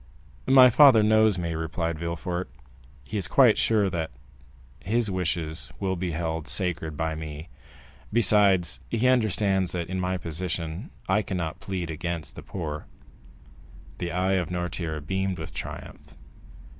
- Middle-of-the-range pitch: No, very low, 90 Hz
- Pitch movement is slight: No, average, 3.4 semitones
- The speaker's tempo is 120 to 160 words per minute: Yes, average, 140 wpm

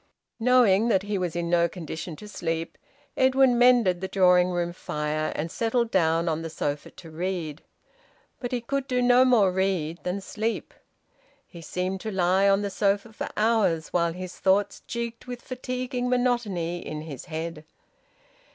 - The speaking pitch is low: No, high, 190 Hz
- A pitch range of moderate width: No, wide, 5.7 semitones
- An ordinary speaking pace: Yes, average, 160 wpm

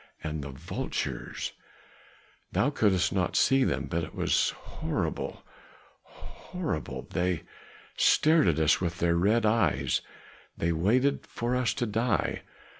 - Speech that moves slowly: Yes, slow, 125 wpm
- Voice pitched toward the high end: No, very low, 95 Hz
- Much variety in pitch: Yes, wide, 6.8 semitones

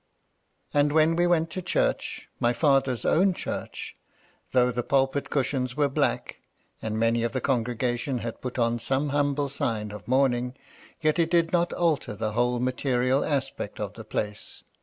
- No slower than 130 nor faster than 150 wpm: No, average, 175 wpm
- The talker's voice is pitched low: Yes, low, 130 Hz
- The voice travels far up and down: No, average, 3.4 semitones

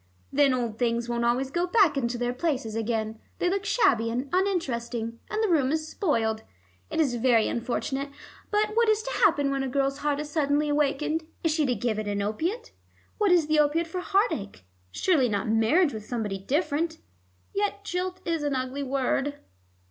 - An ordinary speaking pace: Yes, average, 190 wpm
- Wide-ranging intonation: Yes, wide, 6.3 semitones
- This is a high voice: Yes, very high, 280 Hz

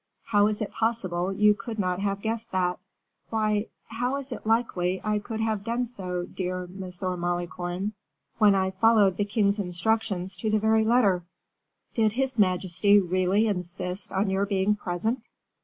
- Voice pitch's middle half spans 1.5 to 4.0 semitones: Yes, average, 3.2 semitones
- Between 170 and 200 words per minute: No, average, 160 wpm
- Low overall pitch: No, high, 200 Hz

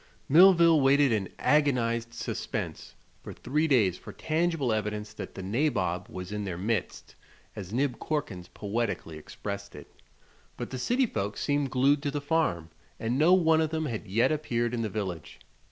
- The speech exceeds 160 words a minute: Yes, average, 170 wpm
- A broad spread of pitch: Yes, wide, 6.8 semitones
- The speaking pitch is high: No, low, 120 Hz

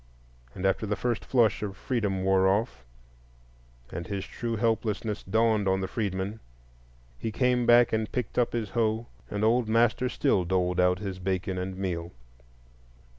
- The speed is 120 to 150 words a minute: No, average, 160 wpm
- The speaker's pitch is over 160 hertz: No, low, 105 Hz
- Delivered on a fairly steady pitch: No, average, 3.4 semitones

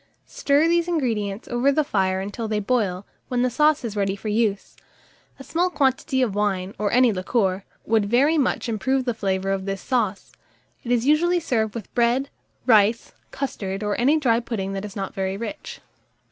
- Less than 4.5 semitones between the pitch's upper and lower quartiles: No, average, 4.9 semitones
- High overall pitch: Yes, high, 230 Hz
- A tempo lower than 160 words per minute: No, average, 185 wpm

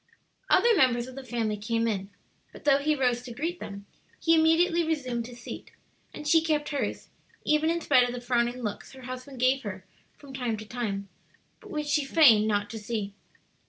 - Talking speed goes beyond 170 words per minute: Yes, average, 195 wpm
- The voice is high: Yes, very high, 255 Hz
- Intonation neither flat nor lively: Yes, average, 4.7 semitones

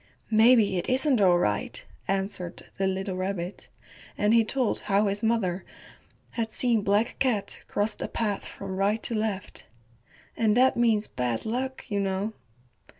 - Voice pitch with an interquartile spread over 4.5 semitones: No, average, 3.0 semitones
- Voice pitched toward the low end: No, high, 205 Hz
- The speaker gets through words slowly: No, average, 150 wpm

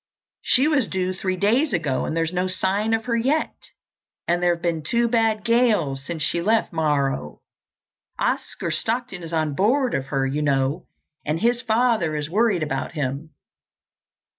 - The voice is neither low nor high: Yes, medium, 180 Hz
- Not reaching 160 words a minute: No, average, 165 wpm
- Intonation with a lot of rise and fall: Yes, wide, 7.0 semitones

